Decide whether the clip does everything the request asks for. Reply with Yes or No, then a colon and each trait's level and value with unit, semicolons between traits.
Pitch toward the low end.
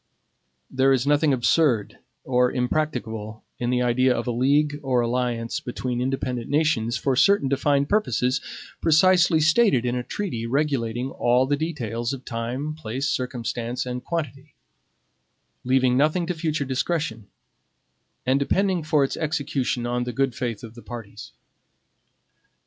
Yes: low, 130 Hz